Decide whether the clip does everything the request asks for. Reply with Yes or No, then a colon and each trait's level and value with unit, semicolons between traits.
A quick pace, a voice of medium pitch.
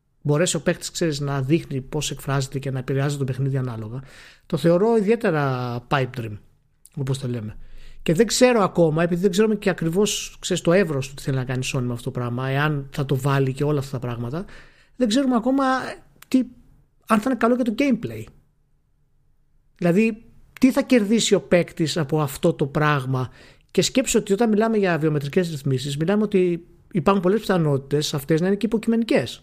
Yes: fast, 185 wpm; medium, 155 Hz